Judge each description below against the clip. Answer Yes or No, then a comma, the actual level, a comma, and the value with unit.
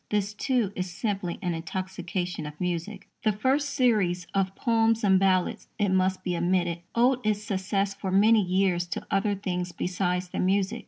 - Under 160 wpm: No, average, 170 wpm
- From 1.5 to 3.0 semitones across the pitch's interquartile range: Yes, average, 2.7 semitones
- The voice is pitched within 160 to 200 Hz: Yes, high, 190 Hz